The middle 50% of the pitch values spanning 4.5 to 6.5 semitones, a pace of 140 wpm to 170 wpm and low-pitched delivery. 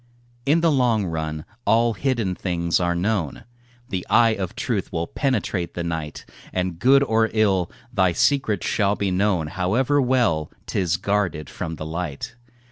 Yes: average, 4.9 semitones; average, 155 wpm; very low, 95 Hz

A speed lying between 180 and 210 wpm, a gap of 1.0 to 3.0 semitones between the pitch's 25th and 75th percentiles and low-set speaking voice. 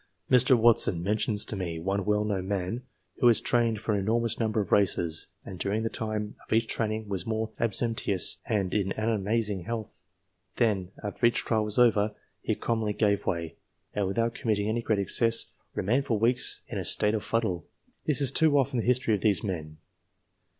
Yes: average, 190 wpm; narrow, 2.6 semitones; low, 110 Hz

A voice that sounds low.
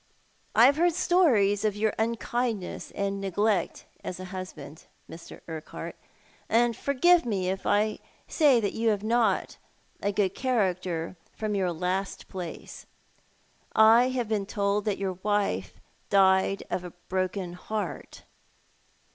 No: high, 200 Hz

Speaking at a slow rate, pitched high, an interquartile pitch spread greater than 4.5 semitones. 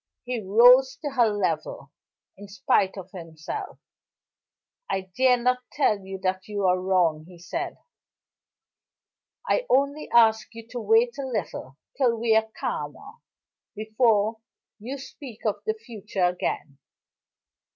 Yes: slow, 130 wpm; high, 220 Hz; average, 5.1 semitones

